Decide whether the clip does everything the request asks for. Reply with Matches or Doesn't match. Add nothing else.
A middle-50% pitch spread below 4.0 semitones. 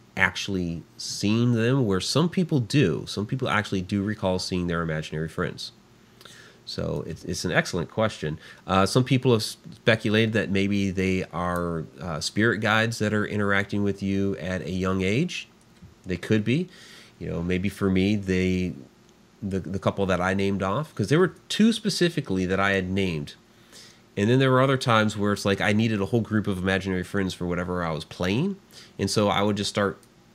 Matches